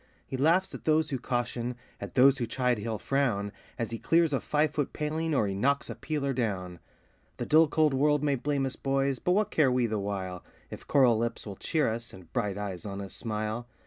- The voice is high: No, low, 125 Hz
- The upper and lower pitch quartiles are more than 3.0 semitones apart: Yes, wide, 5.4 semitones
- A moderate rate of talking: No, fast, 220 wpm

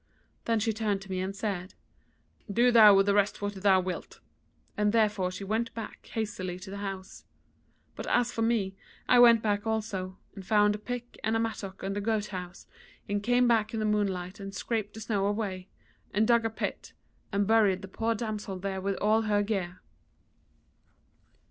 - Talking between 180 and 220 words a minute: Yes, average, 190 wpm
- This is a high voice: Yes, high, 205 Hz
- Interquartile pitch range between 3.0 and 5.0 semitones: No, narrow, 2.4 semitones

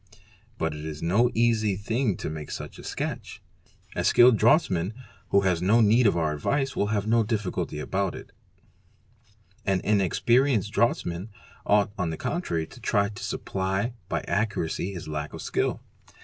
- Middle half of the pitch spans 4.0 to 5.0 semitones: Yes, average, 4.7 semitones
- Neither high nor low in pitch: No, low, 100 Hz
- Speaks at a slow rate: No, average, 165 wpm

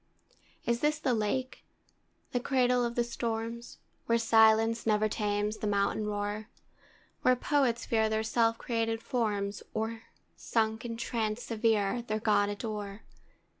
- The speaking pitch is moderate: No, high, 225 Hz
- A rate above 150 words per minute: No, slow, 135 wpm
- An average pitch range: No, narrow, 1.8 semitones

